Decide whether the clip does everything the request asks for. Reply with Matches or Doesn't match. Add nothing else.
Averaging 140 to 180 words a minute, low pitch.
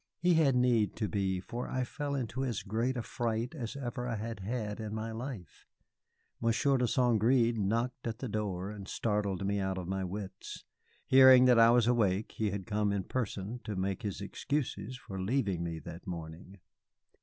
Doesn't match